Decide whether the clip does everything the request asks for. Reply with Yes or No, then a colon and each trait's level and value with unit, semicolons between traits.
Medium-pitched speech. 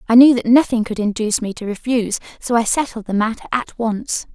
No: high, 230 Hz